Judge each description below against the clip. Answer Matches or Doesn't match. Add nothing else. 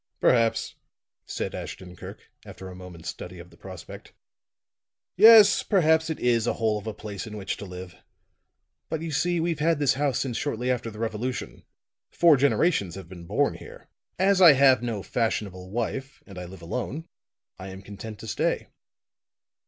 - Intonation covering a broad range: Matches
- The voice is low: Matches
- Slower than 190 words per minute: Matches